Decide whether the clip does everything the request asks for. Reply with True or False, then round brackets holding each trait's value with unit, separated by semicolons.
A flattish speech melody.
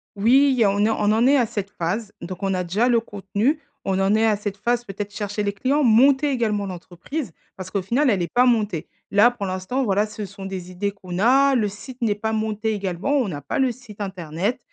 False (3.9 semitones)